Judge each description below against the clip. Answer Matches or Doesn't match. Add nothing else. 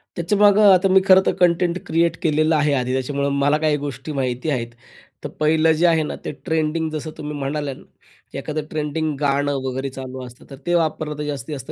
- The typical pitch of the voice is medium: Matches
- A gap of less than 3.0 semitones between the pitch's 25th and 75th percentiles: Matches